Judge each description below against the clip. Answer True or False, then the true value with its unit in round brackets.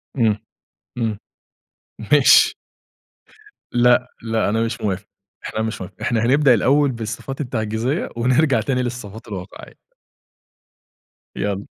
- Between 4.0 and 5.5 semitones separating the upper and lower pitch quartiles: False (2.8 semitones)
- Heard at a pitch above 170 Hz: False (115 Hz)